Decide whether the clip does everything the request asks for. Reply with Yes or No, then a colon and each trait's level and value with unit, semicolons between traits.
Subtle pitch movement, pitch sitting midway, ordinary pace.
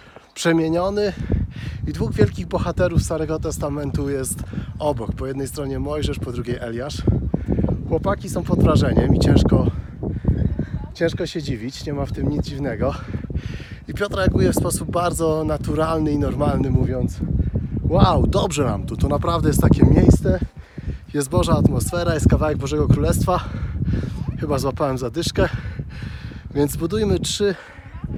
No: average, 4.4 semitones; medium, 145 Hz; average, 135 wpm